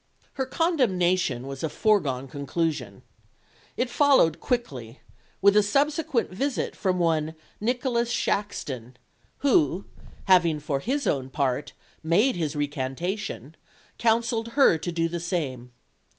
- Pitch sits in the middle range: Yes, medium, 175 Hz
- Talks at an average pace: No, slow, 120 wpm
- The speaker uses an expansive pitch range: Yes, wide, 8.1 semitones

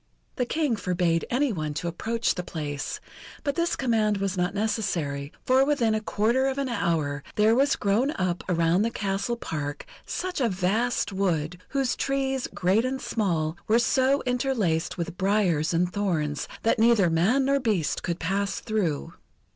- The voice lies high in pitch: Yes, high, 205 Hz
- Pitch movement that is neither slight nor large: No, wide, 6.2 semitones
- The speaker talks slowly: No, average, 165 wpm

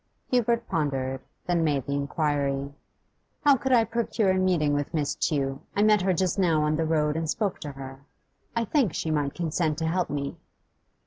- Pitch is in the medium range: Yes, medium, 160 Hz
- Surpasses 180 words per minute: Yes, average, 190 wpm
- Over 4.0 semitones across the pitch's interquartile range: Yes, average, 4.7 semitones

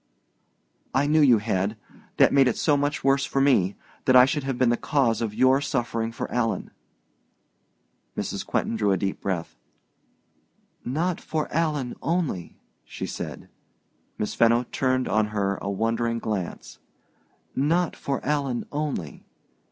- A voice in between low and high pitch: No, low, 125 Hz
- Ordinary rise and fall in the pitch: Yes, average, 4.6 semitones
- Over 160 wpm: No, average, 145 wpm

